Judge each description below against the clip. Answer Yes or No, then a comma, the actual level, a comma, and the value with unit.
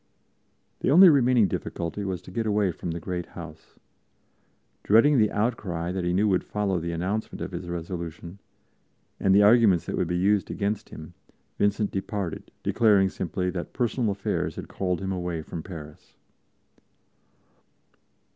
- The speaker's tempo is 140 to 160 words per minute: Yes, average, 150 wpm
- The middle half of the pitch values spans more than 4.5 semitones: No, average, 3.3 semitones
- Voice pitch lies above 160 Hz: No, very low, 95 Hz